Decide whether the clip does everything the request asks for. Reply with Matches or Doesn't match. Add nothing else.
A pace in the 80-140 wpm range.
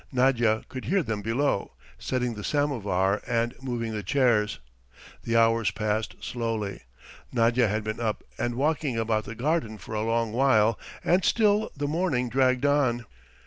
Doesn't match